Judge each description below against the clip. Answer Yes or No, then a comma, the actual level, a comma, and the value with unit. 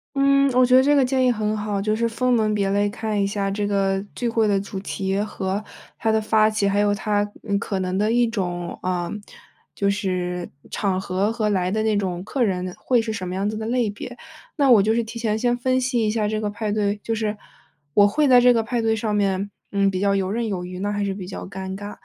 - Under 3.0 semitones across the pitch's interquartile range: Yes, narrow, 2.5 semitones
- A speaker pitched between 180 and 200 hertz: No, high, 210 Hz